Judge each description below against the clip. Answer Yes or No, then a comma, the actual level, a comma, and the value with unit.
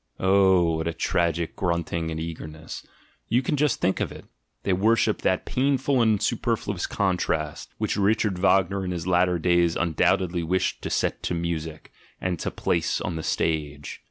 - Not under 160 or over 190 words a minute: Yes, average, 180 wpm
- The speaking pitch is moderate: No, very low, 90 Hz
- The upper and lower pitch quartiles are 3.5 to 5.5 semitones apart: No, average, 3.0 semitones